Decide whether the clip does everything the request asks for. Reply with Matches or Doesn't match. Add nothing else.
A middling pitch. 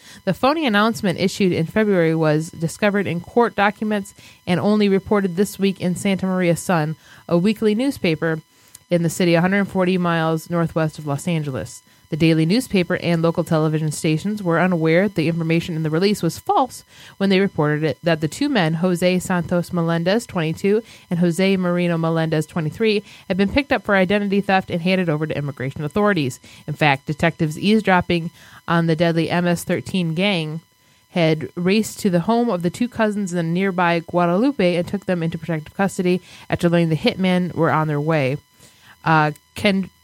Matches